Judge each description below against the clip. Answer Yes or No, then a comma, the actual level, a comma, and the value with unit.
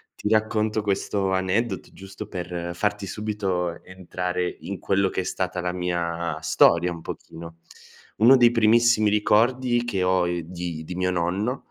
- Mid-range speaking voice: No, very low, 95 Hz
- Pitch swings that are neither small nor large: Yes, average, 3.4 semitones